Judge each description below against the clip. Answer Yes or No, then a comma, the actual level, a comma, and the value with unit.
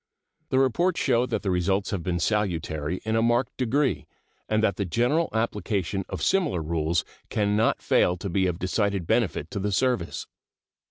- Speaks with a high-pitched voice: No, low, 100 Hz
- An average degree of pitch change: Yes, average, 4.9 semitones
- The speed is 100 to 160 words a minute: No, average, 175 wpm